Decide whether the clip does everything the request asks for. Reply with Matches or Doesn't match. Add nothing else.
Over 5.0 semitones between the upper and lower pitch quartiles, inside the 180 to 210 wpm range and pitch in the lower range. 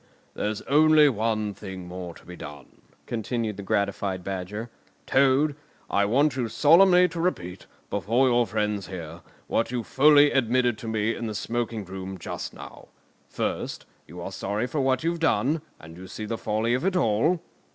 Doesn't match